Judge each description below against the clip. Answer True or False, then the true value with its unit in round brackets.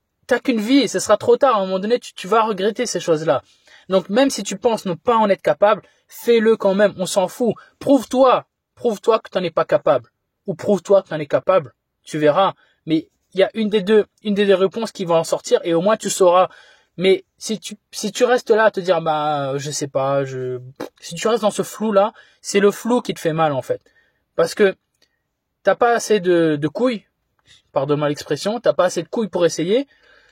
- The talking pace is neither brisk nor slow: False (235 wpm)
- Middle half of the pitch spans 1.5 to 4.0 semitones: False (4.8 semitones)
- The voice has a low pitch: False (200 Hz)